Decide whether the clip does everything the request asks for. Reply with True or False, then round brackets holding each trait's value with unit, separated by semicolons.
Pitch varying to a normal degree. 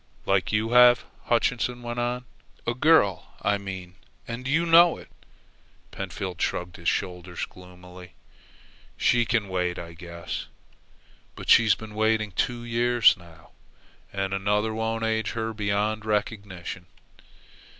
True (4.4 semitones)